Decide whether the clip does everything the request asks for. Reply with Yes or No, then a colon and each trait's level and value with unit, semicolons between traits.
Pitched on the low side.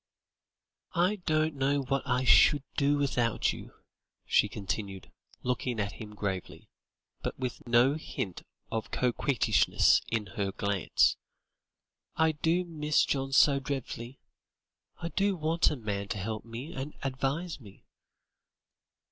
Yes: low, 130 Hz